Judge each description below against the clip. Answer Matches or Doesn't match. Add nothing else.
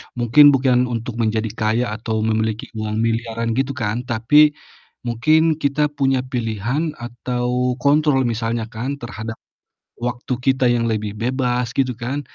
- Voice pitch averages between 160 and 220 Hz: Doesn't match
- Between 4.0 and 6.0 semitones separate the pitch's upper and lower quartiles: Doesn't match